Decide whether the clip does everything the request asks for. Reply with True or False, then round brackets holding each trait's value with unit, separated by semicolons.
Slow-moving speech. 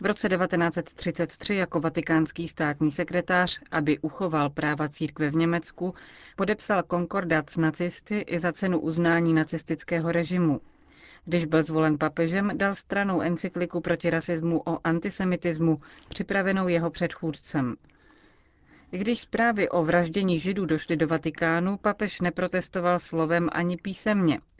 False (125 wpm)